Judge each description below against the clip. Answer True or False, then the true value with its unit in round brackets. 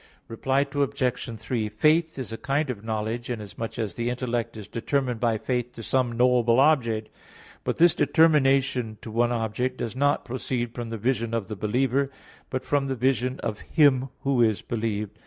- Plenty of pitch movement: False (2.9 semitones)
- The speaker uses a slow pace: False (175 wpm)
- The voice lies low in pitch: True (120 Hz)